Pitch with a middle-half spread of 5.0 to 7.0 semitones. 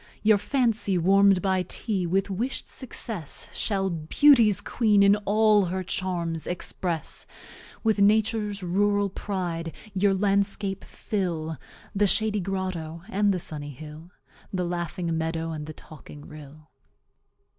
No: average, 3.6 semitones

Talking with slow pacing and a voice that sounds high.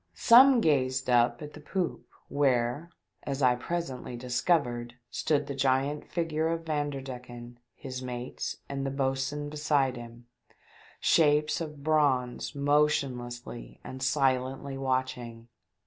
No: slow, 115 wpm; low, 135 Hz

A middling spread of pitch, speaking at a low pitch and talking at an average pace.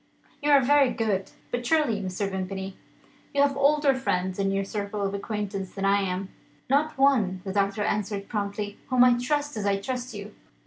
No: average, 5.0 semitones; high, 205 Hz; average, 185 wpm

